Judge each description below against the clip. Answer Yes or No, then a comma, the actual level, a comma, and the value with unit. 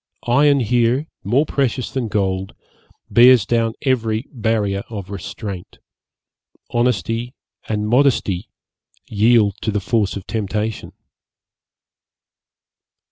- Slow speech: Yes, slow, 95 wpm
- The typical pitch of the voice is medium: No, low, 110 Hz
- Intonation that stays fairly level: No, average, 3.3 semitones